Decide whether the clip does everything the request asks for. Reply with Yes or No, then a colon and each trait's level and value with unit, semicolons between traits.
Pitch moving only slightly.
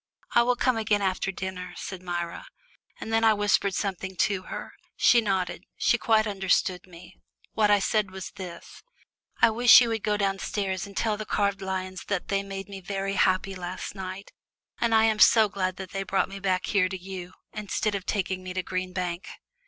Yes: narrow, 2.1 semitones